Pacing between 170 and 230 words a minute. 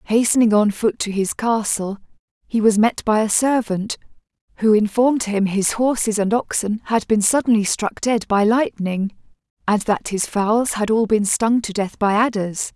Yes: average, 180 wpm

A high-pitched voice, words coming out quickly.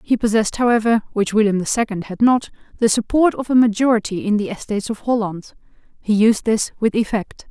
No: high, 220 Hz; average, 190 wpm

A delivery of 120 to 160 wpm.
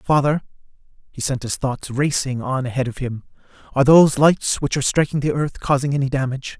No: average, 190 wpm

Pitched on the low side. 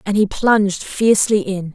No: high, 205 Hz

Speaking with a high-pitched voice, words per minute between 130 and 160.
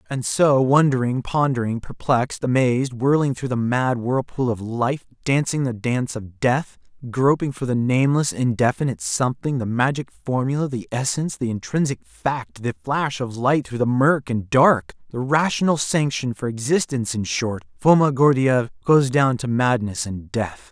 No: low, 130 Hz; average, 155 wpm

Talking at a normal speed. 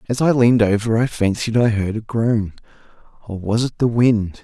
Yes: average, 190 wpm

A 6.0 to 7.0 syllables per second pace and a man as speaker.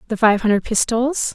No: 6.1 syllables/s; female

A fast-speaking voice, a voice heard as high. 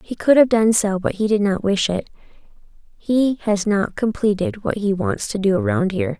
Yes: fast, 215 wpm; high, 205 Hz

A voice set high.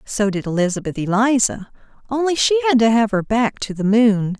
Yes: high, 225 Hz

